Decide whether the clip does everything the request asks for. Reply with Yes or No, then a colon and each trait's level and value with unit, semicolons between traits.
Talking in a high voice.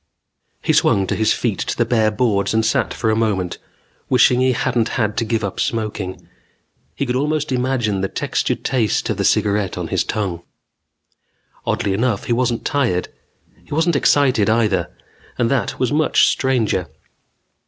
No: low, 115 Hz